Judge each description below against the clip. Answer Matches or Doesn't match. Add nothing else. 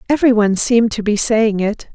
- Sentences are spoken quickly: Doesn't match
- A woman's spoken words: Matches